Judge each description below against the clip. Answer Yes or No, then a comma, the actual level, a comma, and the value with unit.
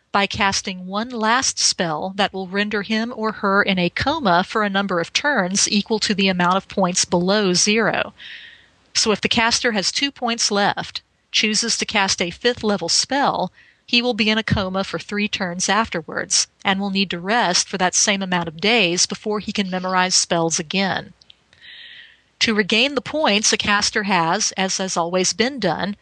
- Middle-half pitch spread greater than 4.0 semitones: No, average, 3.2 semitones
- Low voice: No, high, 205 Hz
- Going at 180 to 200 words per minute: Yes, average, 185 wpm